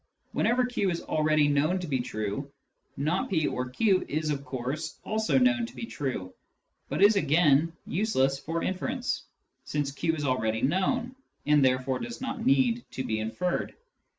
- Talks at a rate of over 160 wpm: Yes, average, 175 wpm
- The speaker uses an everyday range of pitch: No, wide, 7.9 semitones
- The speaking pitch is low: No, medium, 155 Hz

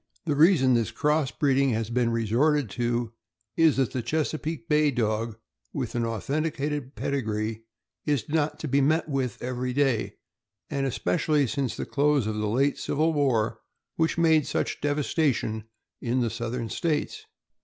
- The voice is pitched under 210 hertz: Yes, low, 135 Hz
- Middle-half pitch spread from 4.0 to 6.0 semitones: Yes, average, 4.4 semitones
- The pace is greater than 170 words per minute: No, average, 155 wpm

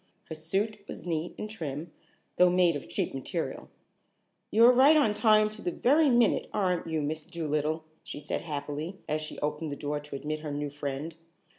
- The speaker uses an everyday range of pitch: No, wide, 5.8 semitones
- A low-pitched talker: No, medium, 160 Hz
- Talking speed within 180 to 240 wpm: Yes, average, 185 wpm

